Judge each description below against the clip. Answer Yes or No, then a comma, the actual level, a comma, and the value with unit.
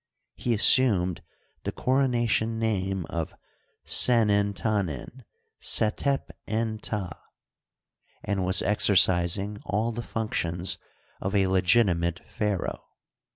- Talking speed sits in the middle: No, slow, 105 wpm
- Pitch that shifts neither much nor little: Yes, average, 3.4 semitones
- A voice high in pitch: No, low, 100 Hz